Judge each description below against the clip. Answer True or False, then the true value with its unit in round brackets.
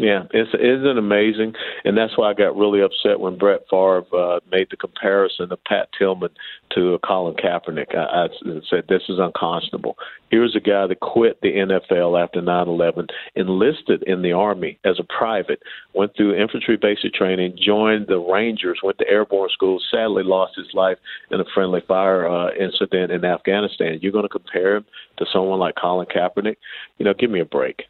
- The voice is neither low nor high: False (95 Hz)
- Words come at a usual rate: True (190 wpm)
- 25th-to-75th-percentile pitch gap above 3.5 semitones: False (2.5 semitones)